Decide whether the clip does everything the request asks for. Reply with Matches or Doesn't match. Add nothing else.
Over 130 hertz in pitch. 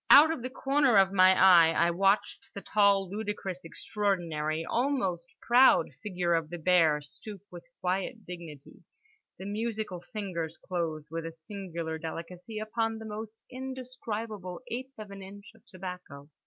Matches